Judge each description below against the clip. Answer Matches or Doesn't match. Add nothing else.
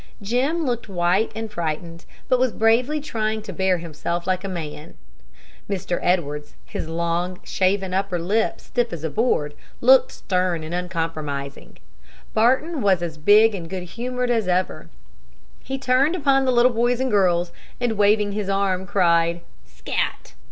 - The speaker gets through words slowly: Doesn't match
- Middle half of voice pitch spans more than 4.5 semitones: Matches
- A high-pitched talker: Matches